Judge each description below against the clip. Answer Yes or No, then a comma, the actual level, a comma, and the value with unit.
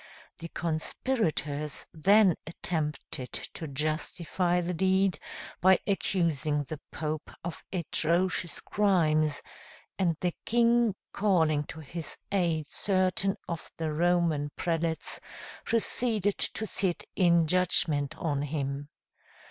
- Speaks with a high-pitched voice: No, medium, 170 Hz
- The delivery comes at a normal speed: No, slow, 105 wpm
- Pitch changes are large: No, average, 3.5 semitones